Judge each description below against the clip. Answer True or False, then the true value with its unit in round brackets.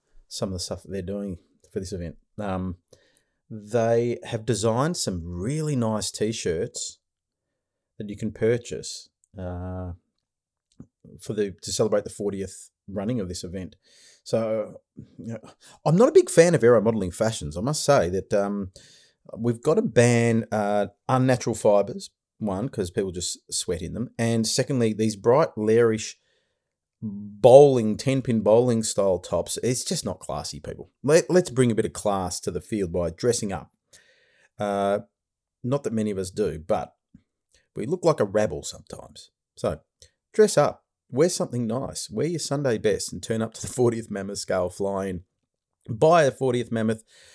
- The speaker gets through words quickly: False (165 wpm)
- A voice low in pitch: True (110 Hz)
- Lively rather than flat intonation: False (3.8 semitones)